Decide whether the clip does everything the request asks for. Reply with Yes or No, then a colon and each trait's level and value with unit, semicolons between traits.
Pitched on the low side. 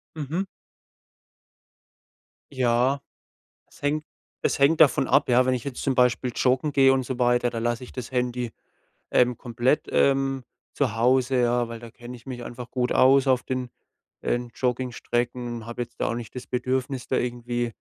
Yes: low, 125 Hz